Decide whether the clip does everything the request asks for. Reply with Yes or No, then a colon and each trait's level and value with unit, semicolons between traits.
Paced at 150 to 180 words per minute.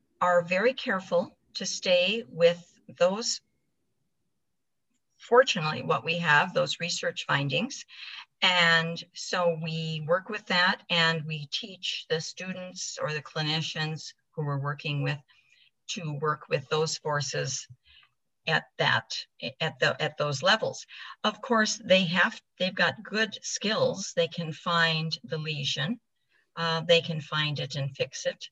No: slow, 135 wpm